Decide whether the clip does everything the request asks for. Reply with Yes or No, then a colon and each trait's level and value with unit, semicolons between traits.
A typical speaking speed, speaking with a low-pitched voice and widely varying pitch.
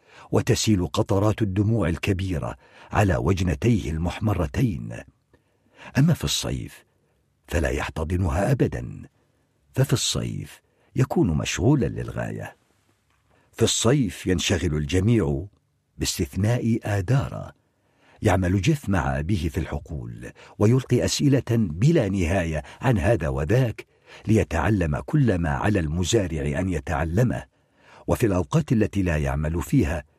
Yes: average, 100 wpm; low, 100 Hz; wide, 5.8 semitones